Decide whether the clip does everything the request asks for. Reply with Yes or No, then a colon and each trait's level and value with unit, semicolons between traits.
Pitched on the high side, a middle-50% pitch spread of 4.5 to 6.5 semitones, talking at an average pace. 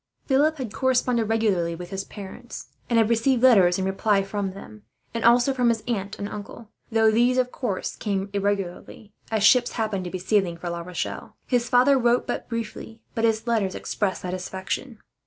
No: high, 220 Hz; average, 3.8 semitones; average, 185 wpm